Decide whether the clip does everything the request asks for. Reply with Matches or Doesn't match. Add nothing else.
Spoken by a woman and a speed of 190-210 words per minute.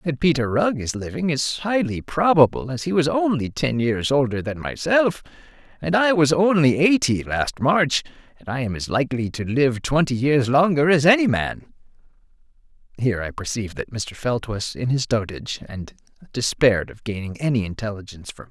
Doesn't match